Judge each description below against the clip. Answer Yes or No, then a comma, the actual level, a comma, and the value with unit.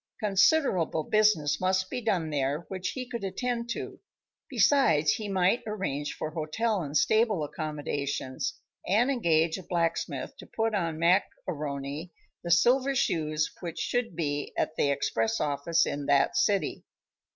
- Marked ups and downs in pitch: Yes, wide, 6.0 semitones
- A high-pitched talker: No, medium, 170 Hz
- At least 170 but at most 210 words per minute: No, average, 145 wpm